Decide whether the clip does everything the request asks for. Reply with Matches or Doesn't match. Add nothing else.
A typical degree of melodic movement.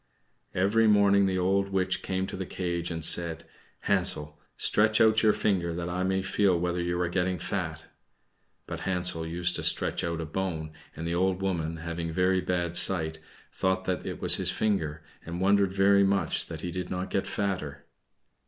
Doesn't match